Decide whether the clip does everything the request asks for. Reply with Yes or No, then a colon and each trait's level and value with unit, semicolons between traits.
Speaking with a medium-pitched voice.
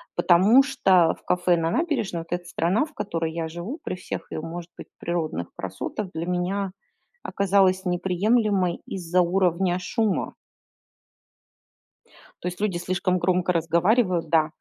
Yes: medium, 180 Hz